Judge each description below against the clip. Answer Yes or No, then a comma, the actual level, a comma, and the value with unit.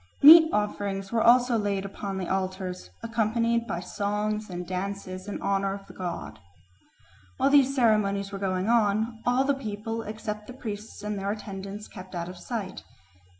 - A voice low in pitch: No, high, 205 Hz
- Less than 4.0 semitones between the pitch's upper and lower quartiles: Yes, average, 2.8 semitones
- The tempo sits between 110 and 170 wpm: Yes, average, 165 wpm